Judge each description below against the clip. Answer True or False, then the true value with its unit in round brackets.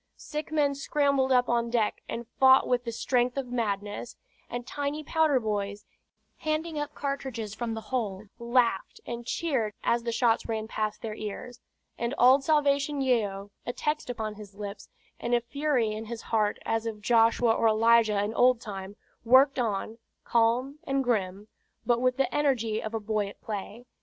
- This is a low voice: False (235 Hz)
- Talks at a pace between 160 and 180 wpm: True (175 wpm)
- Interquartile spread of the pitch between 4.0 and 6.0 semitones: False (3.6 semitones)